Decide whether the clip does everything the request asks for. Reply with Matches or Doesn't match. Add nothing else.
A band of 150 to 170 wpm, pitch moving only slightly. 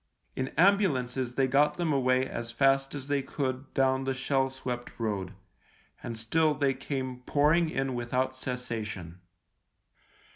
Matches